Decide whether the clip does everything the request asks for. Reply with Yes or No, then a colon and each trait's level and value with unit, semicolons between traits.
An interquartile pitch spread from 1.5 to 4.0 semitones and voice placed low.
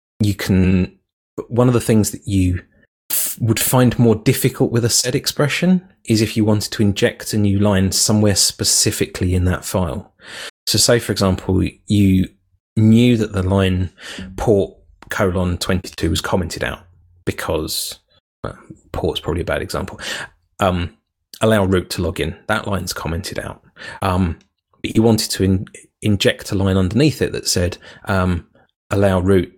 Yes: average, 3.5 semitones; low, 100 Hz